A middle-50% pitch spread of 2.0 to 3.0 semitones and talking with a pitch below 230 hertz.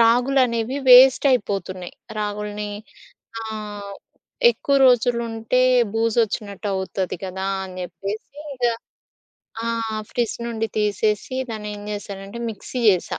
Yes: average, 2.7 semitones; high, 215 Hz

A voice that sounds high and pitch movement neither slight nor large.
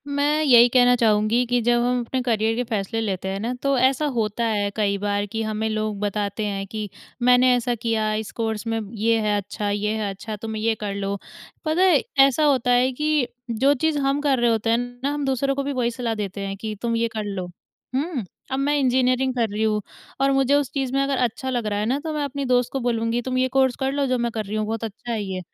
Yes: high, 235 Hz; average, 3.6 semitones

